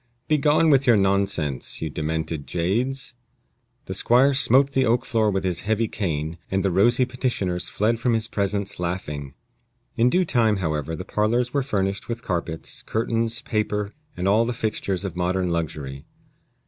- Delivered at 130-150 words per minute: No, average, 160 wpm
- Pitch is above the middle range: No, low, 100 Hz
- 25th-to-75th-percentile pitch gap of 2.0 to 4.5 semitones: No, average, 5.2 semitones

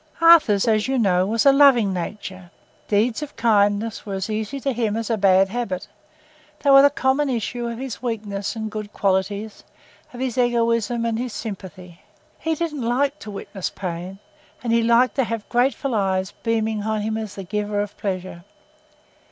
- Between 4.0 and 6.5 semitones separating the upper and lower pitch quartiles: No, average, 3.4 semitones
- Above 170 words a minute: Yes, average, 180 wpm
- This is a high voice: Yes, high, 220 Hz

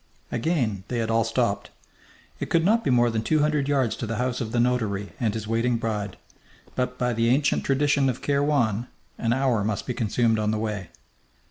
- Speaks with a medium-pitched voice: No, low, 120 Hz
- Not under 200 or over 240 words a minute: Yes, fast, 205 wpm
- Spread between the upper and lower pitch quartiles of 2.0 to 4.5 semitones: Yes, average, 3.4 semitones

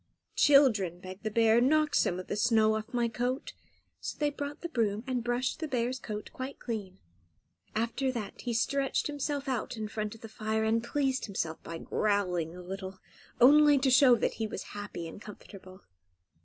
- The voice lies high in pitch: Yes, high, 230 Hz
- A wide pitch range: No, average, 4.3 semitones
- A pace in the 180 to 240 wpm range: Yes, average, 185 wpm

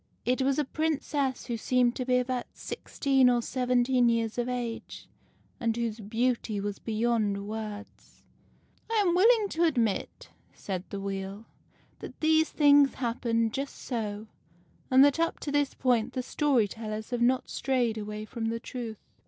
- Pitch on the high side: Yes, high, 240 Hz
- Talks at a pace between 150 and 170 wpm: Yes, average, 165 wpm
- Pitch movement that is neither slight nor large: Yes, average, 3.3 semitones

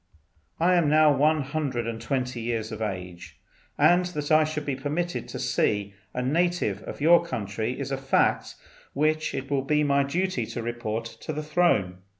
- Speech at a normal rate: Yes, average, 180 wpm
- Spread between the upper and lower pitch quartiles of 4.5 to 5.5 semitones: Yes, average, 5.0 semitones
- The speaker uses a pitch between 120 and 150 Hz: Yes, medium, 140 Hz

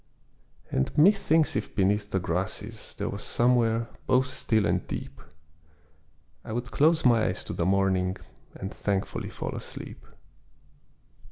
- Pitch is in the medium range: No, low, 110 Hz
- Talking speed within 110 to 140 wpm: Yes, slow, 135 wpm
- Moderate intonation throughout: Yes, average, 4.7 semitones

